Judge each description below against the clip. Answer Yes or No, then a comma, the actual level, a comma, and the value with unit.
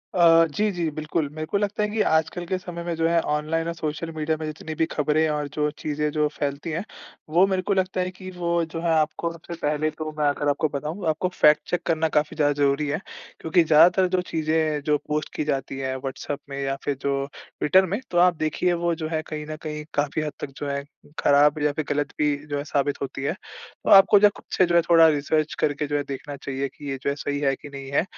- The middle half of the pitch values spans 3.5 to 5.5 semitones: No, narrow, 2.6 semitones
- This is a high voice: No, medium, 155 Hz